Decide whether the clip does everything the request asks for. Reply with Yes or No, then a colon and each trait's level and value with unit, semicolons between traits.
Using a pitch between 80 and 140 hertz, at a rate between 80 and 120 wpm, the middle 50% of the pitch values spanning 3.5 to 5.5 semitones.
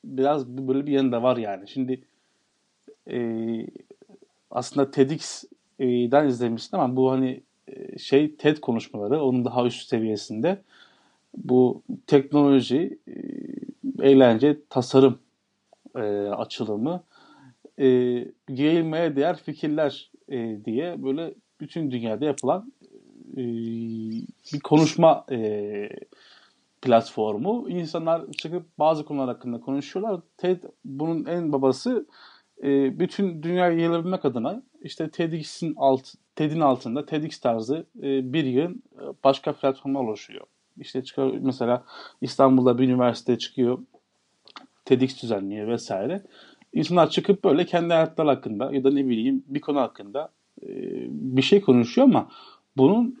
Yes: low, 135 Hz; average, 115 wpm; average, 4.6 semitones